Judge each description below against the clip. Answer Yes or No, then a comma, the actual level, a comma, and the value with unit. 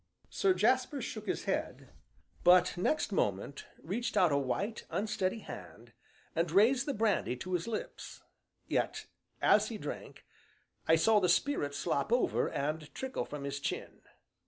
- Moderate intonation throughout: No, wide, 7.3 semitones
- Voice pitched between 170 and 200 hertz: Yes, medium, 185 Hz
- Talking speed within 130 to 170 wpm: Yes, average, 150 wpm